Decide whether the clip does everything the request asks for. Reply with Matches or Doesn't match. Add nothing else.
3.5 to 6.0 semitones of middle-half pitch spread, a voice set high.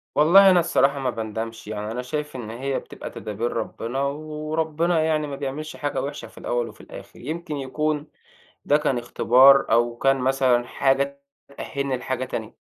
Doesn't match